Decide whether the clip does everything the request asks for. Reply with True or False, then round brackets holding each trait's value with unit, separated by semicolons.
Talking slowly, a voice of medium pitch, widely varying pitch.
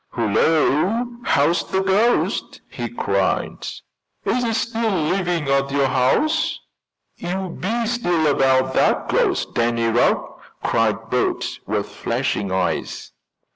True (115 wpm; 160 Hz; 8.8 semitones)